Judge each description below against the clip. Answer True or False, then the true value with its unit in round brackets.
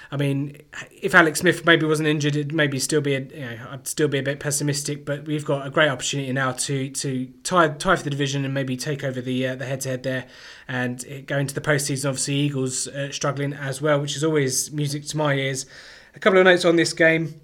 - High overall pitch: False (140 Hz)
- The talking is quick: True (240 wpm)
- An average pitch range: False (2.1 semitones)